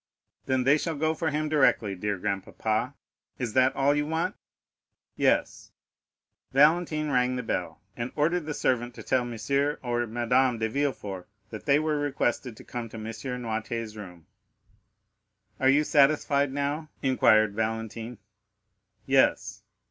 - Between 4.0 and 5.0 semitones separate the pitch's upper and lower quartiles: Yes, average, 4.5 semitones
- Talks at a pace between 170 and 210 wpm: No, average, 140 wpm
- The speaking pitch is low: Yes, low, 125 Hz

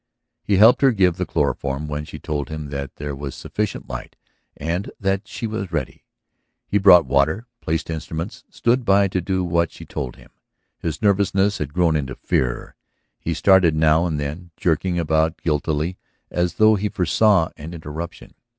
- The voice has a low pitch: Yes, very low, 85 Hz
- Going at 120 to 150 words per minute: No, average, 170 wpm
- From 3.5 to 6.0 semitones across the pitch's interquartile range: Yes, average, 4.3 semitones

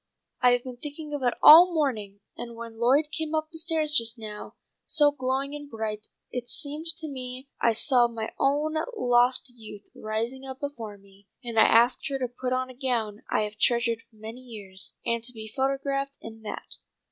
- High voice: Yes, very high, 250 Hz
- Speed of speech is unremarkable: Yes, average, 190 wpm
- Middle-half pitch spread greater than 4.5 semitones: No, average, 4.0 semitones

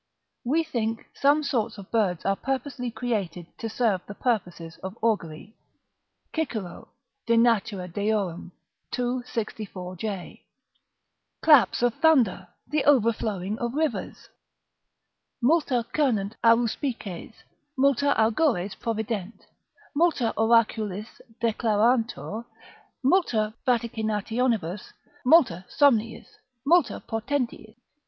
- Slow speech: Yes, slow, 90 wpm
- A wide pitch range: No, average, 3.5 semitones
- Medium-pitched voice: No, high, 225 Hz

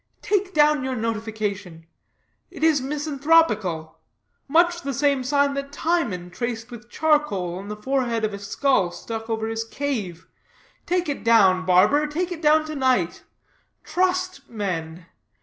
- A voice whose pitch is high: Yes, very high, 255 Hz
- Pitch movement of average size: No, wide, 6.6 semitones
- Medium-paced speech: Yes, average, 145 wpm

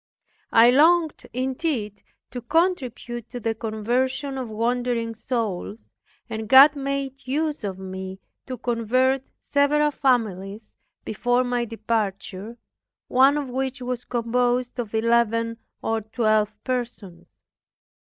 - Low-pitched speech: No, high, 240 Hz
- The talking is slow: Yes, slow, 115 wpm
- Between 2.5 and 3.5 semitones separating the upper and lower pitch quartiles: Yes, average, 3.0 semitones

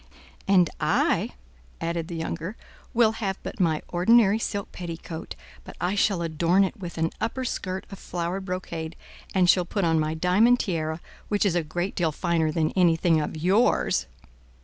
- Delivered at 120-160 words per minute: No, average, 170 wpm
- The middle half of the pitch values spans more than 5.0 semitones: No, average, 3.2 semitones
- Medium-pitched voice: Yes, medium, 175 Hz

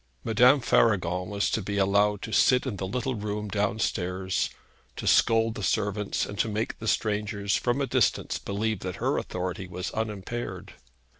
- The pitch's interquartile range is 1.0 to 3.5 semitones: Yes, narrow, 2.4 semitones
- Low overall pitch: Yes, low, 105 Hz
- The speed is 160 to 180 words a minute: Yes, average, 165 wpm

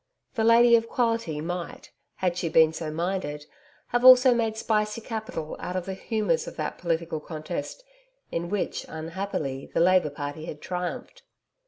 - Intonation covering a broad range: Yes, wide, 5.7 semitones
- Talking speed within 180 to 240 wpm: No, average, 160 wpm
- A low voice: No, medium, 180 Hz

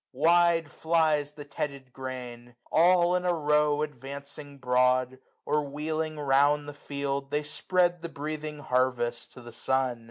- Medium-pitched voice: Yes, medium, 145 Hz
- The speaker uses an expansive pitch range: No, average, 3.0 semitones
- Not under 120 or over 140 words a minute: No, average, 150 wpm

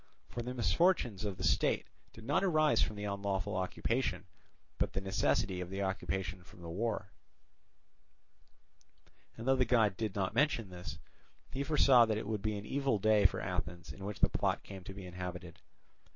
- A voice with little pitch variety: No, average, 4.0 semitones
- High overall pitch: No, low, 100 Hz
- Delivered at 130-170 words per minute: No, average, 180 wpm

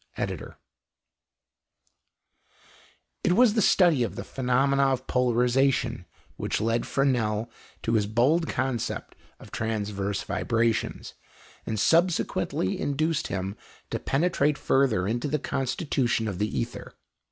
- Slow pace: Yes, slow, 115 wpm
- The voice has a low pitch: Yes, low, 125 Hz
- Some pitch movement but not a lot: Yes, average, 4.1 semitones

